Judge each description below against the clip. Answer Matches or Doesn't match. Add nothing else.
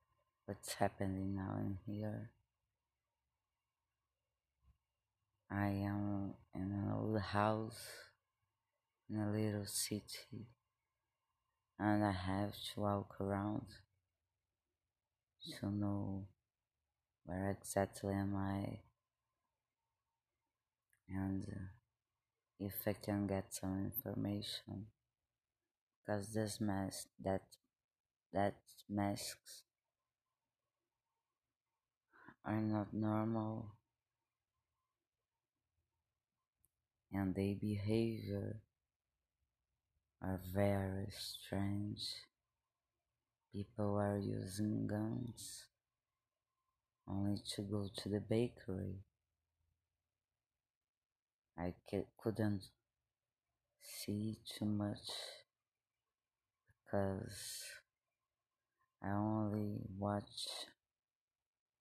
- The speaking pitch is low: Matches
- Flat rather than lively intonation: Matches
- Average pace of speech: Doesn't match